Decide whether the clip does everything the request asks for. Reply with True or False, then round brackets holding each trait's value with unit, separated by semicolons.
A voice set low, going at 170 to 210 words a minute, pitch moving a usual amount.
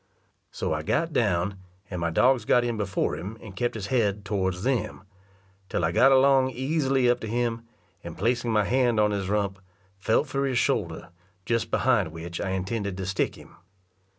True (110 Hz; 185 wpm; 4.4 semitones)